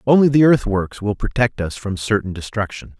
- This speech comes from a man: Yes, male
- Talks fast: No, average, 180 wpm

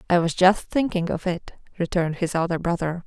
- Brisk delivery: No, average, 195 wpm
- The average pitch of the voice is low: No, medium, 175 Hz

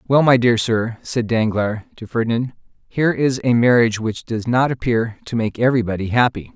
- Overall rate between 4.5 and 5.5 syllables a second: Yes, 5.3 syllables/s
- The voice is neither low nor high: No, low, 120 Hz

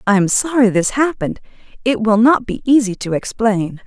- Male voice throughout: No, female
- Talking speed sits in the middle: Yes, average, 185 wpm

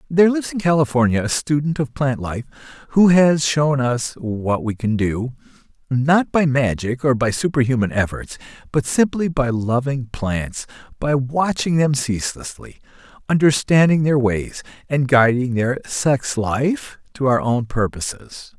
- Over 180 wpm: No, average, 145 wpm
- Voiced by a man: Yes, male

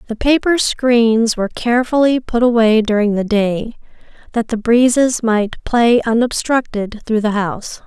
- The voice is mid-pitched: No, high, 230 Hz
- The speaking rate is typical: Yes, average, 145 wpm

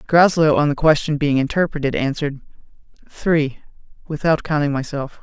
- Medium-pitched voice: Yes, medium, 145 Hz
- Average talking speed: No, slow, 125 wpm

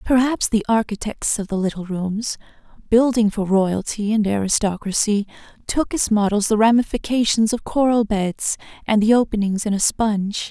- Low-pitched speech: No, high, 215 Hz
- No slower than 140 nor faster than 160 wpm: Yes, average, 150 wpm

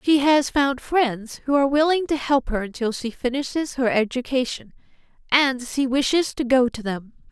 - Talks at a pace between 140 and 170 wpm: No, average, 180 wpm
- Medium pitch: No, very high, 265 Hz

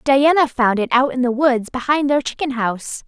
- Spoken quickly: Yes, fast, 215 wpm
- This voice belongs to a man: No, female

